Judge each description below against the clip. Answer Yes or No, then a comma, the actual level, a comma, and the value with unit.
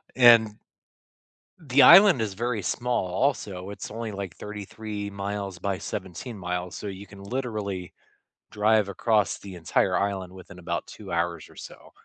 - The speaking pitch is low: Yes, low, 100 Hz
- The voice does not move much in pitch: No, average, 3.1 semitones